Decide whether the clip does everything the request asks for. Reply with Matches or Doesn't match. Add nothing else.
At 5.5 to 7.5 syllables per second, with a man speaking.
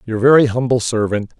Matches